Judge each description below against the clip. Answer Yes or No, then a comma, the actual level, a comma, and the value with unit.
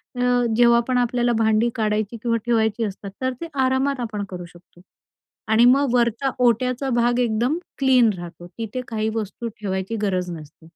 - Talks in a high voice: Yes, high, 230 Hz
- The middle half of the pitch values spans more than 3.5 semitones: No, average, 2.9 semitones